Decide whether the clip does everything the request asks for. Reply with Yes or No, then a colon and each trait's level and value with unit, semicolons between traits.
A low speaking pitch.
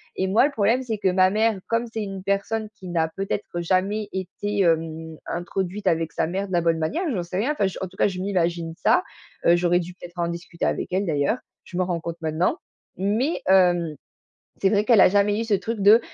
No: high, 190 Hz